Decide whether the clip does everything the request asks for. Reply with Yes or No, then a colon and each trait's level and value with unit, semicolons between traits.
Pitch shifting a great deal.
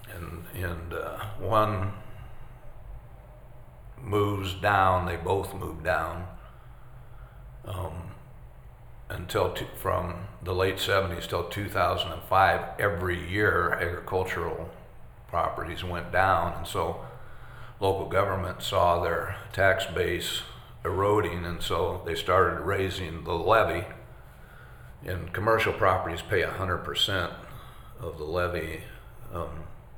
No: average, 4.4 semitones